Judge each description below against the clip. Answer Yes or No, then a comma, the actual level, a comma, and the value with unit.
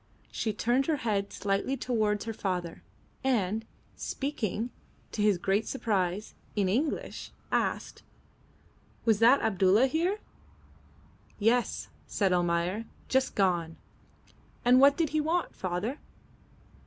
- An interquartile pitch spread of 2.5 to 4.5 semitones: No, average, 5.2 semitones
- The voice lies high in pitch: Yes, high, 220 Hz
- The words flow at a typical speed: No, slow, 115 wpm